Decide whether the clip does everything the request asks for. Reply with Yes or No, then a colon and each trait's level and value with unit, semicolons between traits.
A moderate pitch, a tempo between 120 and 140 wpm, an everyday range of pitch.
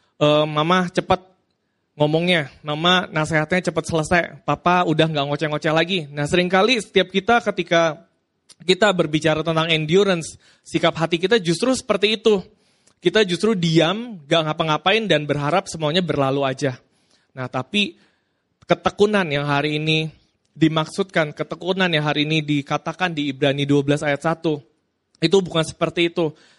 Yes: medium, 165 Hz; average, 130 wpm; average, 3.7 semitones